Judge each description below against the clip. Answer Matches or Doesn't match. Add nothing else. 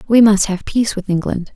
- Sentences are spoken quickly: Matches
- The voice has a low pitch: Doesn't match